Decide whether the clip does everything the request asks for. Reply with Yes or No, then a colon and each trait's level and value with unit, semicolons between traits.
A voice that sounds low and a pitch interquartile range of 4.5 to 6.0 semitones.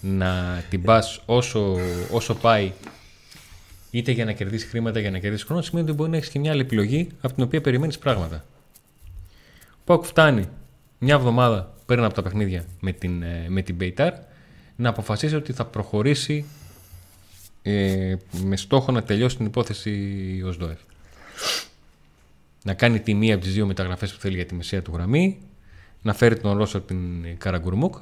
Yes: low, 105 Hz; average, 4.9 semitones